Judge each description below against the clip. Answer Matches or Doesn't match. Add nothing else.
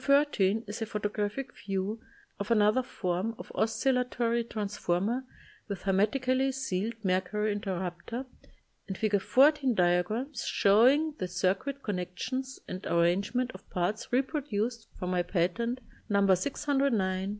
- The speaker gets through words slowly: Matches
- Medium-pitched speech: Doesn't match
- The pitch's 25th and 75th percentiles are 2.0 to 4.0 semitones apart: Doesn't match